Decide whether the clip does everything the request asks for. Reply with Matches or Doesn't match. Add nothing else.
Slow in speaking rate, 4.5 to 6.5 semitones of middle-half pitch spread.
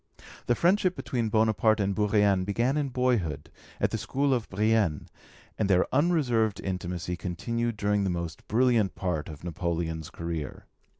Doesn't match